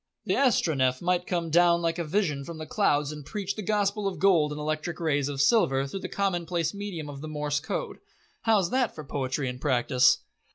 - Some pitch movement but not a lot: Yes, average, 5.0 semitones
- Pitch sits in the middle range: Yes, medium, 160 Hz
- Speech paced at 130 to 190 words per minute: No, fast, 205 wpm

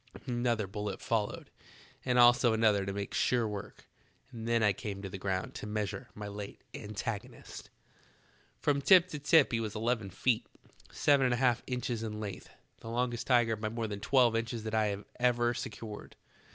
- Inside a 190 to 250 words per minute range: No, average, 180 wpm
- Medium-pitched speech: No, low, 115 Hz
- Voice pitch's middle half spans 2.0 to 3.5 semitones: Yes, average, 2.8 semitones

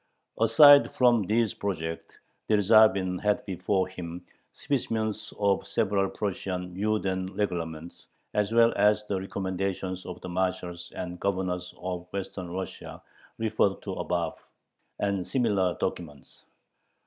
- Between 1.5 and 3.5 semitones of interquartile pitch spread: Yes, average, 2.7 semitones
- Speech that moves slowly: Yes, slow, 115 wpm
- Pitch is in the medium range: No, very low, 95 Hz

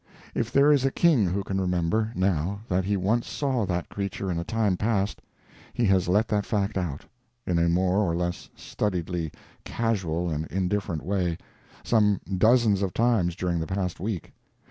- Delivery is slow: No, average, 175 wpm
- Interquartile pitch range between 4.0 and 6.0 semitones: No, average, 3.5 semitones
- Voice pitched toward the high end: No, very low, 95 Hz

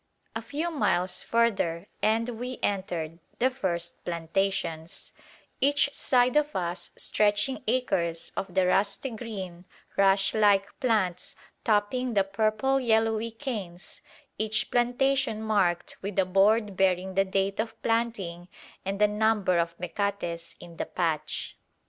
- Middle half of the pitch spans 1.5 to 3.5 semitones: No, average, 4.0 semitones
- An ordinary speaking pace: No, slow, 130 wpm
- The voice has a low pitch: No, high, 205 Hz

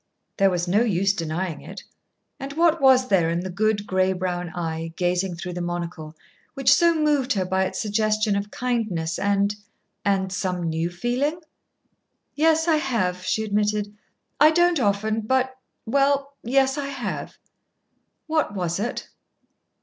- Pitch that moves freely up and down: Yes, wide, 6.7 semitones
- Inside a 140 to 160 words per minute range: Yes, average, 150 wpm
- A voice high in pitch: Yes, high, 205 Hz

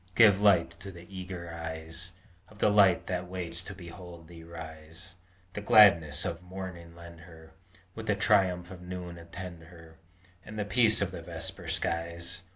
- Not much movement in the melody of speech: Yes, narrow, 2.0 semitones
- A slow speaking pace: No, average, 165 wpm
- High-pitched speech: No, very low, 85 Hz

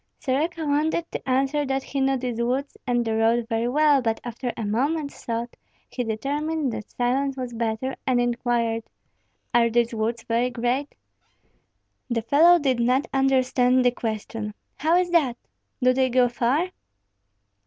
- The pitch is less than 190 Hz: No, very high, 250 Hz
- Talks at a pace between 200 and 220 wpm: No, average, 155 wpm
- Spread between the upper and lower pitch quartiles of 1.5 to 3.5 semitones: Yes, average, 2.9 semitones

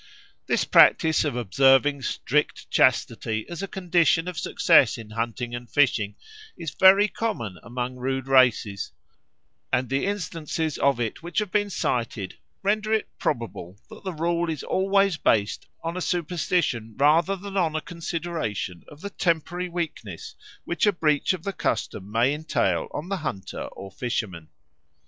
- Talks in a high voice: No, medium, 150 Hz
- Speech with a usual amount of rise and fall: No, wide, 6.8 semitones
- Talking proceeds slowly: No, average, 155 wpm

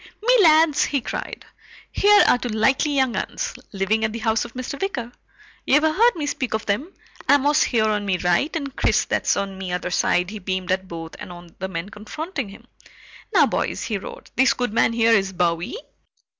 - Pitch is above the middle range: Yes, high, 225 Hz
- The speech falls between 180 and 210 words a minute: Yes, average, 200 wpm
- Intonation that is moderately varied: No, wide, 6.7 semitones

